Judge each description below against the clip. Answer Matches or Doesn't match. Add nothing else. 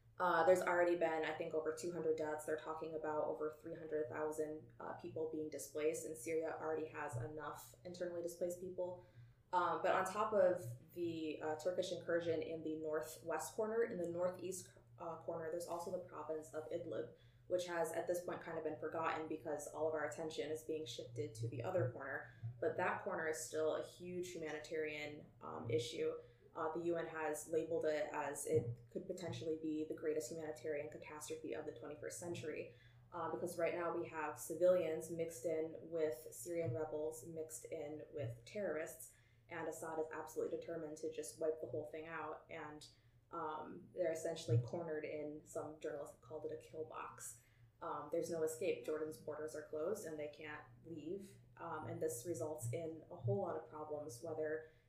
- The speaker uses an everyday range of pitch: Doesn't match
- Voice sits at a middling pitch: Matches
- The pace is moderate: Matches